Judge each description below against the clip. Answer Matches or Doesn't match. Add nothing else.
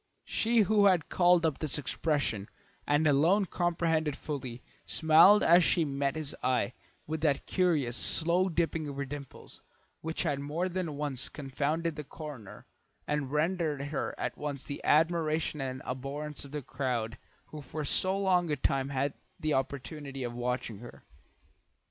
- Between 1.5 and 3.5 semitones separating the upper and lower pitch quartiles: Matches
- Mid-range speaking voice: Matches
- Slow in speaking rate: Doesn't match